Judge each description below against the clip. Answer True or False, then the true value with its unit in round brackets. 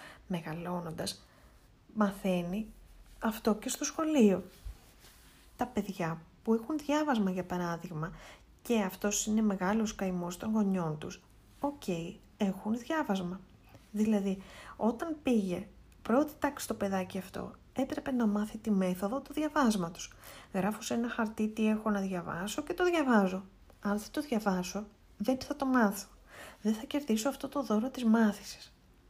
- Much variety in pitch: False (4.6 semitones)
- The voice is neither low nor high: False (210 Hz)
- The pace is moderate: True (140 wpm)